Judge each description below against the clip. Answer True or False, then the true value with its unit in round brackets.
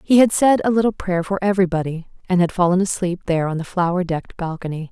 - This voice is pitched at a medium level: True (180 Hz)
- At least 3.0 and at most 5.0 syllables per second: False (6.7 syllables/s)